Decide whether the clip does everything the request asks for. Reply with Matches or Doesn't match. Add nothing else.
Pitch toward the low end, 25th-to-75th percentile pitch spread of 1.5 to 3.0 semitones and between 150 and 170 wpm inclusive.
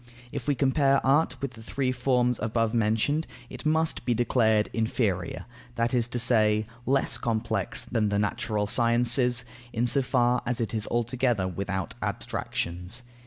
Matches